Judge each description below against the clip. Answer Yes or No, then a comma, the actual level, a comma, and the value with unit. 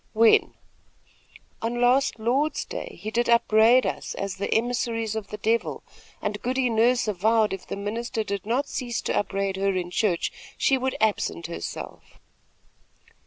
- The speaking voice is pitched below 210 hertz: No, high, 225 Hz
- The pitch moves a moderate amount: Yes, average, 3.0 semitones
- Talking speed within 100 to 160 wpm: Yes, average, 155 wpm